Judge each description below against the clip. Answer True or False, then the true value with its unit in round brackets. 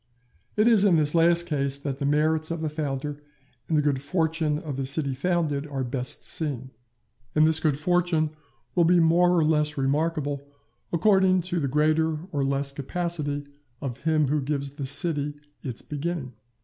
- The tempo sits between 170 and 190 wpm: True (175 wpm)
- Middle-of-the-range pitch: True (150 Hz)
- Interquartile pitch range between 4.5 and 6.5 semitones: False (2.8 semitones)